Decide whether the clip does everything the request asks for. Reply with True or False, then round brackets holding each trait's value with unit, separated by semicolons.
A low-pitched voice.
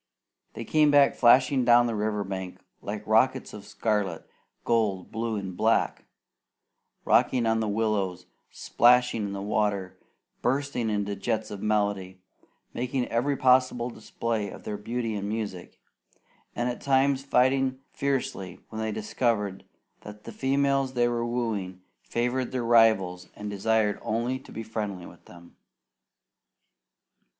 True (110 Hz)